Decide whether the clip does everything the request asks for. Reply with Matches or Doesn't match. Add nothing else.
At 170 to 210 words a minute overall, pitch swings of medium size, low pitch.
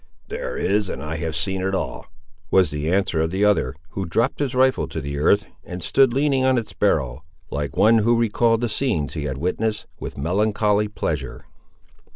Doesn't match